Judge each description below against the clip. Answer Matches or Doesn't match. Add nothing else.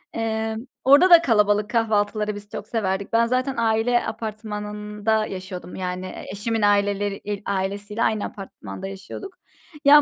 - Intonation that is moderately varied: Doesn't match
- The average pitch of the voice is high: Matches